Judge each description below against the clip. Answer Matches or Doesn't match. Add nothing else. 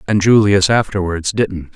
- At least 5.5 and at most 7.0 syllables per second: Doesn't match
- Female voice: Doesn't match